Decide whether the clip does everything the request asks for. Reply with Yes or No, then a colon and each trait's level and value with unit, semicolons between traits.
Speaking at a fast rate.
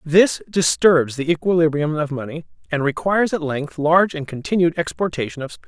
No: average, 170 wpm